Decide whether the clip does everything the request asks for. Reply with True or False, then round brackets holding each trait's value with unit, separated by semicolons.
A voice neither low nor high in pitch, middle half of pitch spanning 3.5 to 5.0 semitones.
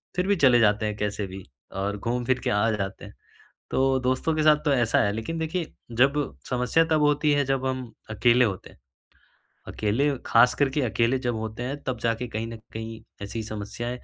False (120 Hz; 3.8 semitones)